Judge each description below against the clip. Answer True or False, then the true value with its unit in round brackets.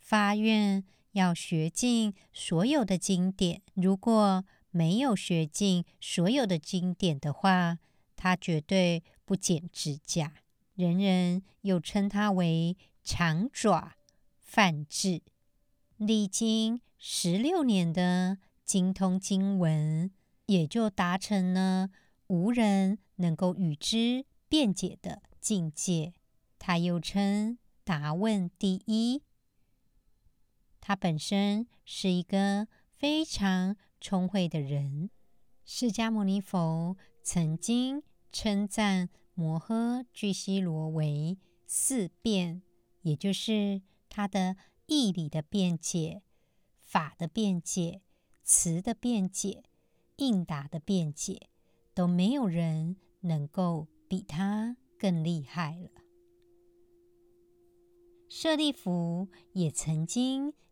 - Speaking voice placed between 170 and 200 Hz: True (190 Hz)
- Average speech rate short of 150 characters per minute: True (140 characters per minute)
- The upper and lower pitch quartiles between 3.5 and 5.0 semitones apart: True (3.8 semitones)